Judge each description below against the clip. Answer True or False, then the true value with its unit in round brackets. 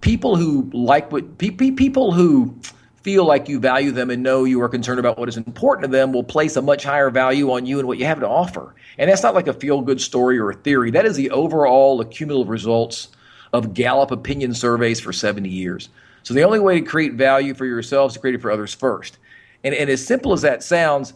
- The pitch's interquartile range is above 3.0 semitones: False (2.6 semitones)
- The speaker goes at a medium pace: False (235 wpm)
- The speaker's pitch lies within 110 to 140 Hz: True (130 Hz)